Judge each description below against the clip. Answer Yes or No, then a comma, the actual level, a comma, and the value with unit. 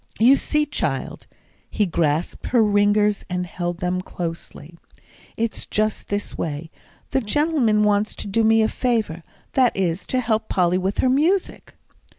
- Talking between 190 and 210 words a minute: No, average, 155 wpm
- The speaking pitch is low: No, high, 210 Hz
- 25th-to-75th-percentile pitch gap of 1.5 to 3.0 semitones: No, average, 4.6 semitones